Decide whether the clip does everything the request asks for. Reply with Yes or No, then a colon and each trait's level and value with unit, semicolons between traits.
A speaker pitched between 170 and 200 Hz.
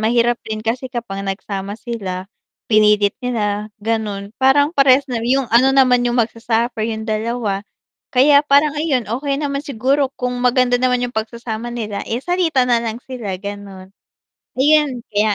No: high, 235 Hz